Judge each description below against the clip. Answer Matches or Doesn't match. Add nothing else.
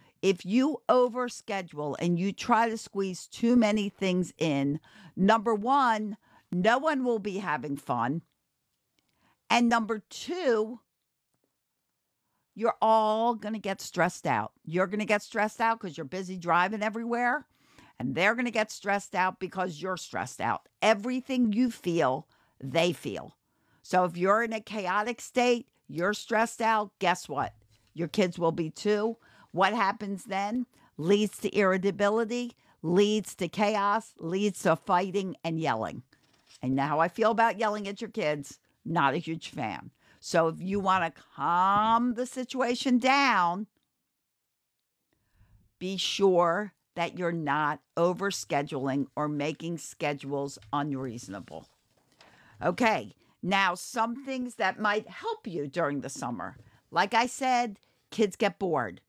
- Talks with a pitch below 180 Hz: Doesn't match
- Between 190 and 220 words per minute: Doesn't match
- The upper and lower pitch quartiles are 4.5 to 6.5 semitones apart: Matches